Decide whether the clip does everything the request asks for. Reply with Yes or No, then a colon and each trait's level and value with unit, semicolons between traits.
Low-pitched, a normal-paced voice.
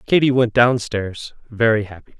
Yes: low, 115 Hz; average, 165 wpm